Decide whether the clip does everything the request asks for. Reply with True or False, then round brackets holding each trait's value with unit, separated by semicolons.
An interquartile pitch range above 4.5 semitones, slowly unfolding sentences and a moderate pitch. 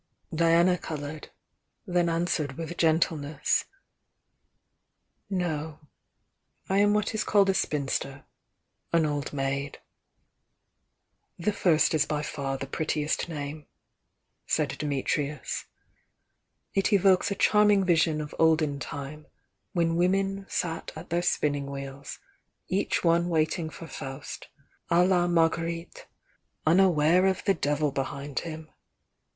False (3.2 semitones; 120 wpm; 160 Hz)